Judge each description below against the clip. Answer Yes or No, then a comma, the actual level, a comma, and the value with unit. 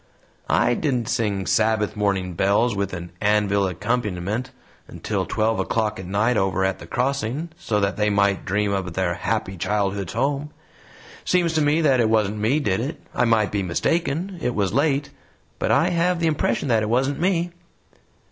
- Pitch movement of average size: No, wide, 5.7 semitones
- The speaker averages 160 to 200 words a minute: Yes, average, 180 wpm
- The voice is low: Yes, low, 110 Hz